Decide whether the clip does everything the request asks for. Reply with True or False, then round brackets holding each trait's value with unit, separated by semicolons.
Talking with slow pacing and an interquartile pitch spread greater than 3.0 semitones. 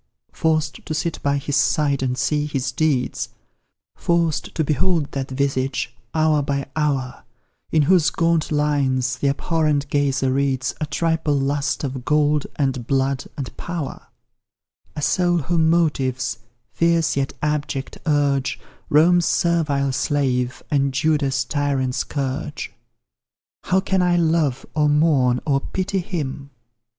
False (130 wpm; 2.7 semitones)